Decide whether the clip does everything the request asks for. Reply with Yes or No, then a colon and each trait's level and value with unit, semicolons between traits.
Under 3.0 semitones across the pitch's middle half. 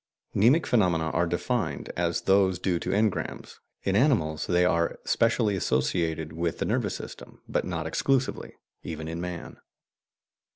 No: average, 3.4 semitones